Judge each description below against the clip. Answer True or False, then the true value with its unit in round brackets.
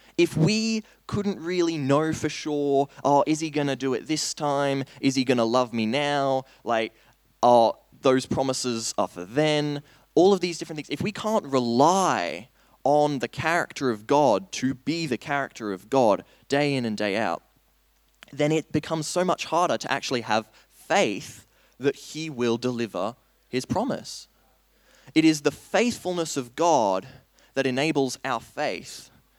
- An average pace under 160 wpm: False (165 wpm)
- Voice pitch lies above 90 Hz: True (140 Hz)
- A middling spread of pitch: True (3.8 semitones)